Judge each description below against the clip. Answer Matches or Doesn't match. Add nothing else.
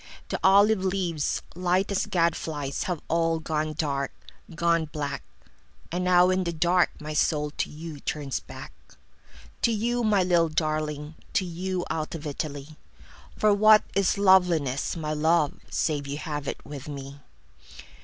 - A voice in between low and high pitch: Matches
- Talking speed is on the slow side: Matches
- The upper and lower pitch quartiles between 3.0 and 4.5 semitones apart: Matches